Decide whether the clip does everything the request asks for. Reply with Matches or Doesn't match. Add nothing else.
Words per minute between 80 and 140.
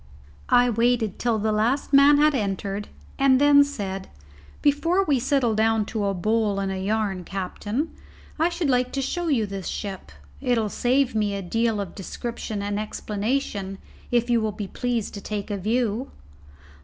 Doesn't match